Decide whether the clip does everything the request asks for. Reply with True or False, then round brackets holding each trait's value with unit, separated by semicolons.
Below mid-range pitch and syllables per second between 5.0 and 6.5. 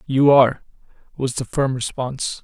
True (130 Hz; 5.1 syllables/s)